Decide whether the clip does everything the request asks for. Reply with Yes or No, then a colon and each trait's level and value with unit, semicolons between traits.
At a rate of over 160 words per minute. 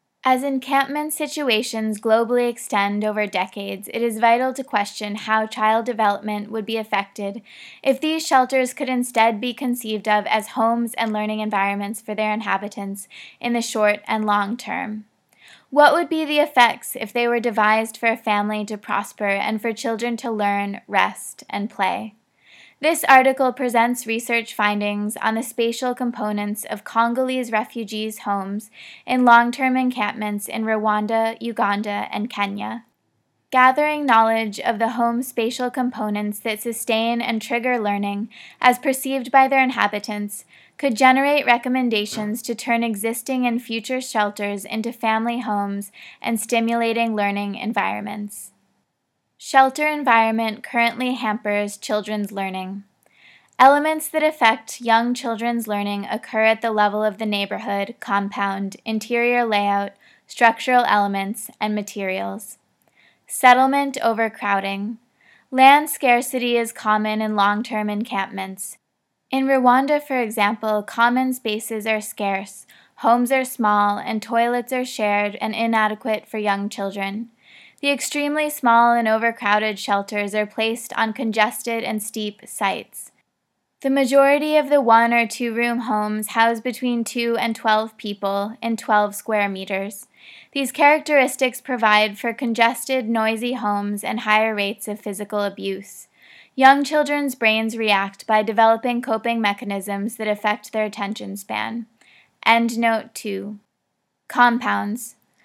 No: slow, 135 wpm